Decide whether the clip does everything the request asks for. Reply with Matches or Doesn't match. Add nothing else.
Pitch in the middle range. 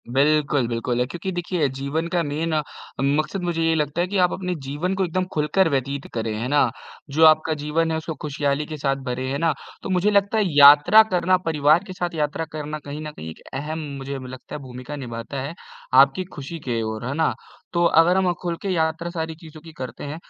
Matches